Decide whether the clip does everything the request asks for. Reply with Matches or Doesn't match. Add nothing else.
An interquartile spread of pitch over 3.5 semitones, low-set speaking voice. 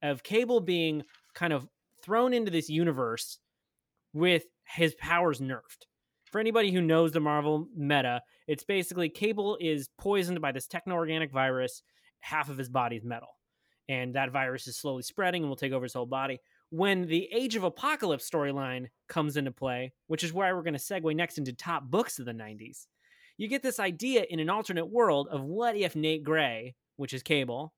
Doesn't match